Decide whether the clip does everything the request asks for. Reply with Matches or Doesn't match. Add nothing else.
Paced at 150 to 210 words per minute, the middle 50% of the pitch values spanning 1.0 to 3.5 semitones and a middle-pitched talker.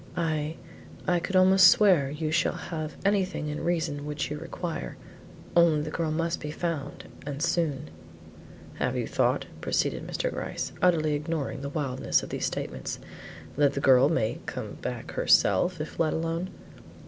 Matches